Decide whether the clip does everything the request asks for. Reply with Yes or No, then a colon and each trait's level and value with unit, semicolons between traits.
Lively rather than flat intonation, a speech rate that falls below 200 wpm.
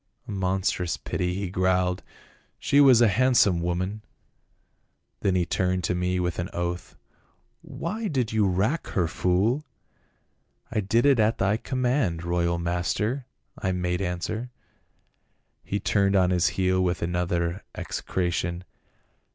No: average, 3.7 semitones; average, 145 wpm